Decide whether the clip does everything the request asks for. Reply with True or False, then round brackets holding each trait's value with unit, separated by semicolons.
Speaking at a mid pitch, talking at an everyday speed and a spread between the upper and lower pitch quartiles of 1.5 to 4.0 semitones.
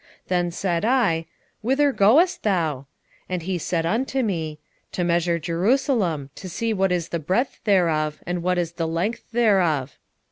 False (180 Hz; 165 wpm; 4.7 semitones)